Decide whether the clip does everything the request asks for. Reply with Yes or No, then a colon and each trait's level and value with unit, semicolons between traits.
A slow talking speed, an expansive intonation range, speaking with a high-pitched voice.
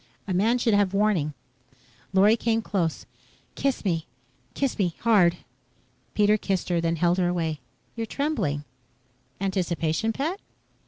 No: slow, 130 wpm; average, 4.7 semitones; high, 195 Hz